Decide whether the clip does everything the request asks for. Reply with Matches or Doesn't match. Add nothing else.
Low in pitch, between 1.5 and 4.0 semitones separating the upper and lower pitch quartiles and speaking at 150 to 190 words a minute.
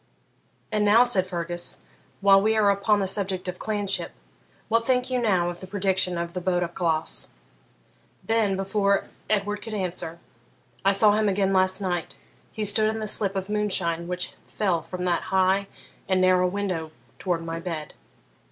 Doesn't match